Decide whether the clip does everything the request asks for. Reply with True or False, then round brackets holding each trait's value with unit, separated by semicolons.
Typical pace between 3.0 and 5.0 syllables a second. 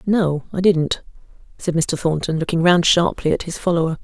False (5.2 syllables/s)